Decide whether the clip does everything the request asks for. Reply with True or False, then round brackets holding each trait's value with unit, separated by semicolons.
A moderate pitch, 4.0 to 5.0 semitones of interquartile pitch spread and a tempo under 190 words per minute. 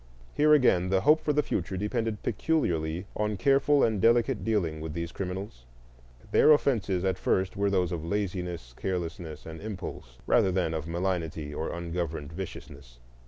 False (90 Hz; 4.4 semitones; 160 wpm)